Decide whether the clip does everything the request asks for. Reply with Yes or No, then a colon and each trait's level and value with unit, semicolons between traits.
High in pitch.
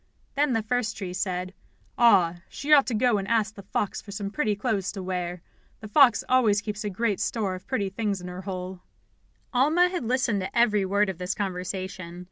Yes: high, 205 Hz